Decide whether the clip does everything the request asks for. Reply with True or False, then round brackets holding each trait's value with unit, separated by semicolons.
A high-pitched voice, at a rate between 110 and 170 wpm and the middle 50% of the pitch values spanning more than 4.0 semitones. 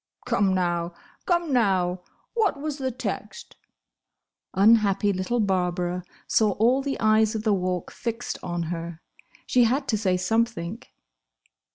True (210 Hz; 135 wpm; 4.8 semitones)